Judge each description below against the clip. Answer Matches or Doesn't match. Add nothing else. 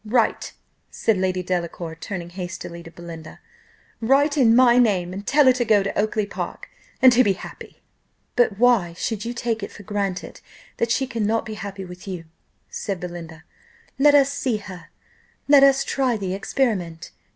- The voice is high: Matches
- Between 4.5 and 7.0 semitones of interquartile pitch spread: Matches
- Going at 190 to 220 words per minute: Doesn't match